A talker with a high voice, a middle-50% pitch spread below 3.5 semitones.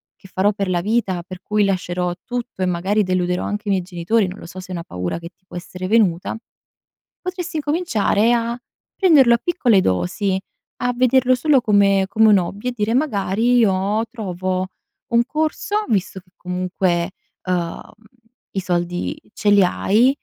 No: high, 200 Hz; average, 4.6 semitones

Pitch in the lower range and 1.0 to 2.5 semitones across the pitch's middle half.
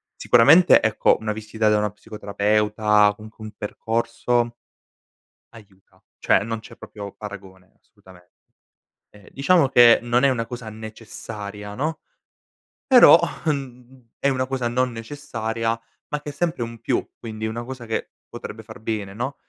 No: low, 115 Hz; average, 2.9 semitones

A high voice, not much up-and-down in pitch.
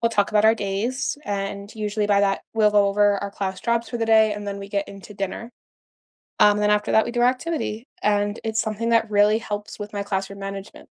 Yes: high, 210 Hz; narrow, 1.8 semitones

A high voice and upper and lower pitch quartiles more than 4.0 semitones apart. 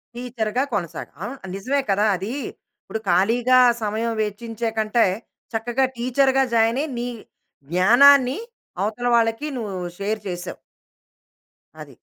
No: high, 230 Hz; average, 3.1 semitones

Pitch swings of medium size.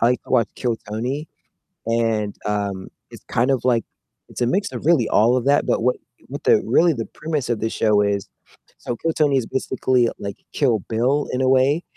Yes: average, 3.5 semitones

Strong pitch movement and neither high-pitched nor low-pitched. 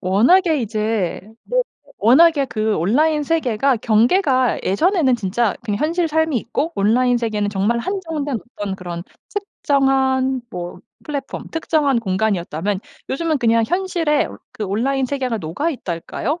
No: wide, 6.3 semitones; very high, 255 Hz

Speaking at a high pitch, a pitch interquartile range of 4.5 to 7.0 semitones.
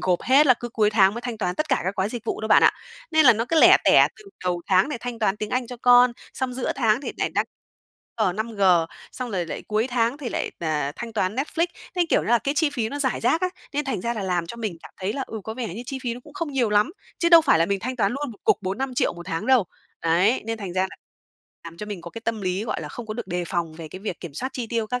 Yes: high, 225 Hz; average, 5.1 semitones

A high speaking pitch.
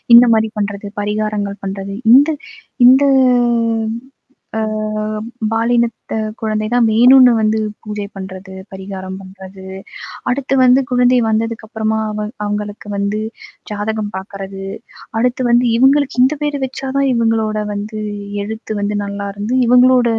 Yes: high, 220 Hz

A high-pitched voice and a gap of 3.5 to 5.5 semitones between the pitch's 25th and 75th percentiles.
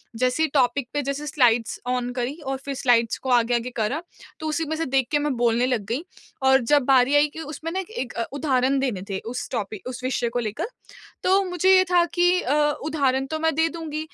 Yes: very high, 270 Hz; average, 4.2 semitones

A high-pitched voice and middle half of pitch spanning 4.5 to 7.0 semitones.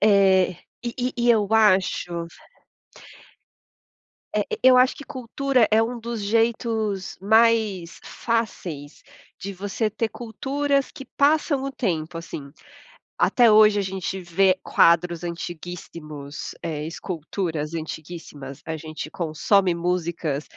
Yes: high, 195 Hz; wide, 5.4 semitones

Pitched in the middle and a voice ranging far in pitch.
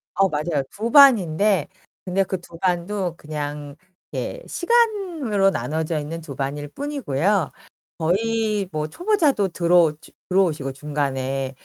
Yes: medium, 175 Hz; wide, 6.1 semitones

